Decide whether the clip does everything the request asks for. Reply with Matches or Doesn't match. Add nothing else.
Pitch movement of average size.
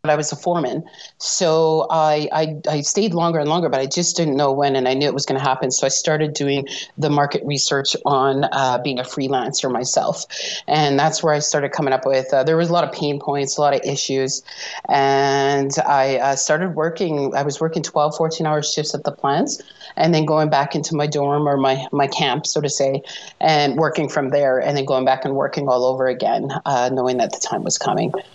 Doesn't match